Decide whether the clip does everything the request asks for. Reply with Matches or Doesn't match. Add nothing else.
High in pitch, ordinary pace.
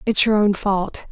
Doesn't match